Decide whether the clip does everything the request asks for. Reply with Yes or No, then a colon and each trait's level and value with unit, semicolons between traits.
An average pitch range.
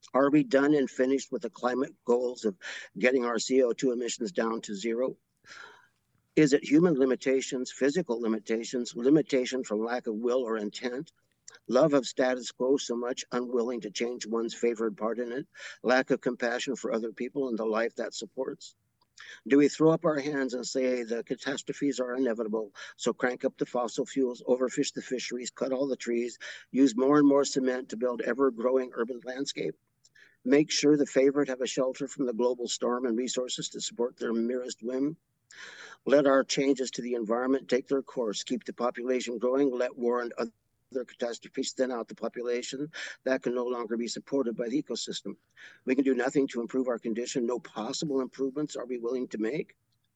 No: narrow, 2.2 semitones